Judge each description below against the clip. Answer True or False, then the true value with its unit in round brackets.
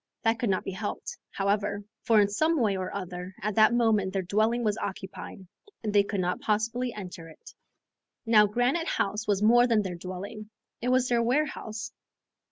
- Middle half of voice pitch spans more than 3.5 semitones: False (3.0 semitones)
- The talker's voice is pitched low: False (210 Hz)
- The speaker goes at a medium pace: True (180 wpm)